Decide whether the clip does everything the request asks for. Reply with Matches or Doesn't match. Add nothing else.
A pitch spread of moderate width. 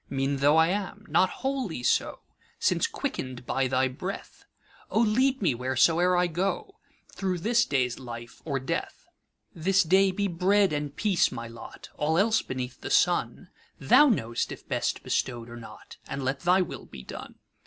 Doesn't match